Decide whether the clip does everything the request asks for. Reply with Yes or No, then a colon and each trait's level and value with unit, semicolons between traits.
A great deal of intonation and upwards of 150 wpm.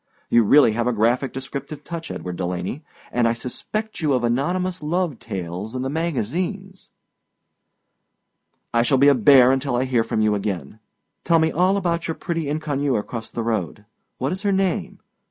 Yes: wide, 6.4 semitones; average, 175 wpm